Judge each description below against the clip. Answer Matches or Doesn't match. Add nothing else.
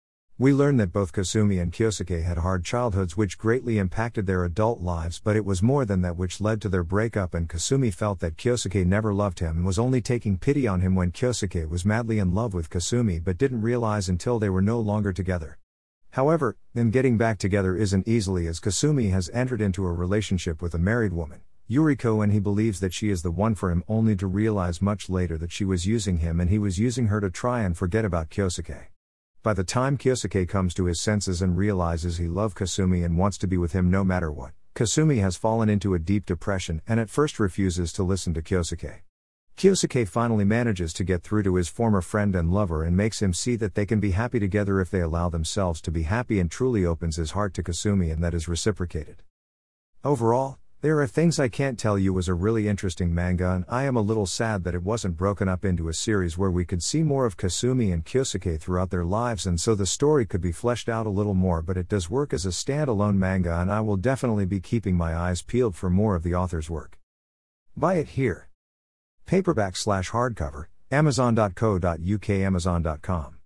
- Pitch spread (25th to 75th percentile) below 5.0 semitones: Matches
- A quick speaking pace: Matches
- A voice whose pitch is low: Matches